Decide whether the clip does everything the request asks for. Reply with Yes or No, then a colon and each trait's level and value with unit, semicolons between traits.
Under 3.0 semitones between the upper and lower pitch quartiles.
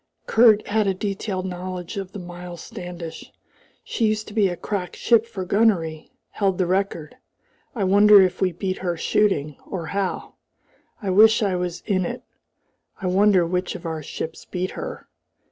Yes: narrow, 2.5 semitones